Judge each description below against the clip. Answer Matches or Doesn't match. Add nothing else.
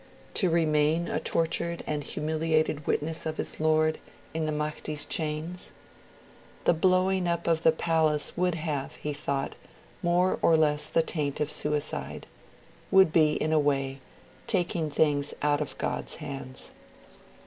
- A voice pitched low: Doesn't match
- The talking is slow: Doesn't match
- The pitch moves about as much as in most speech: Doesn't match